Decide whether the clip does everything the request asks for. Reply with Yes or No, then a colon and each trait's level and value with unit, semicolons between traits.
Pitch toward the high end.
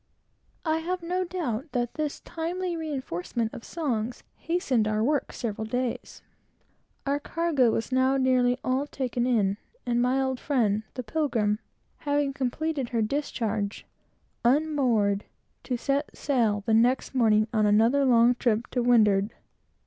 Yes: very high, 250 Hz